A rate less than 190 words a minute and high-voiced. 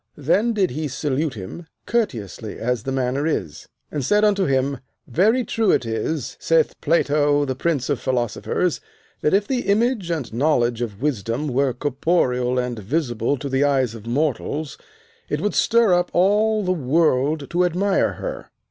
No: average, 165 wpm; medium, 145 Hz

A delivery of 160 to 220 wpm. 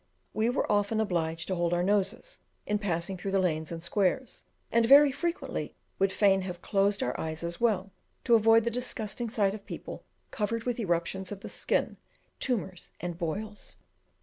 Yes: average, 175 wpm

